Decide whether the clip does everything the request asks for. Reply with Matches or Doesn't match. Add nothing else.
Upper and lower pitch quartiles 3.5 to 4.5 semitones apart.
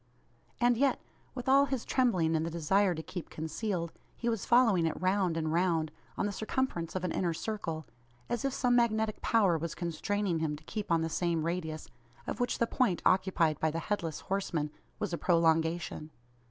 Doesn't match